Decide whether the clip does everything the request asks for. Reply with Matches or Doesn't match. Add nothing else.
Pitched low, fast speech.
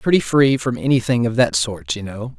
Matches